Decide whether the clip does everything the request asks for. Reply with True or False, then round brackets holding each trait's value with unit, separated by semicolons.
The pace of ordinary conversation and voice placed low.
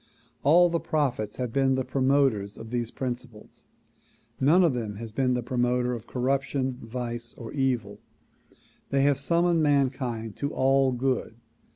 True (155 wpm; 130 Hz)